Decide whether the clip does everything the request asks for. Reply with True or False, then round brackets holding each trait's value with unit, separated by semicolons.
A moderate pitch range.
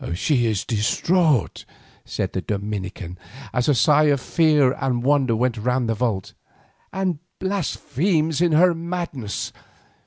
False (6.2 semitones)